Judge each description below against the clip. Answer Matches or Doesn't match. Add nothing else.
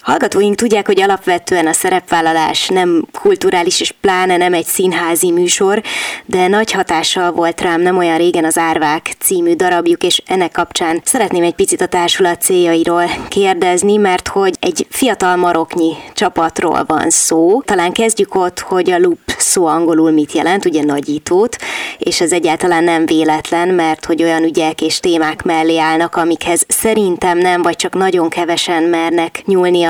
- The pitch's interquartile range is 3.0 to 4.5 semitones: Matches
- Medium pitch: Matches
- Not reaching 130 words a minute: Doesn't match